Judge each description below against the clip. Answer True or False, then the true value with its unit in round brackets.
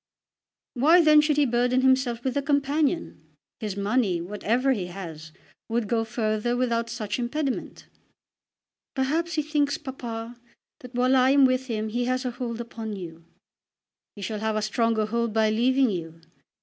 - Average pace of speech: True (160 wpm)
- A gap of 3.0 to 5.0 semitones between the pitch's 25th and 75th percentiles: True (3.4 semitones)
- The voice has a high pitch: True (240 Hz)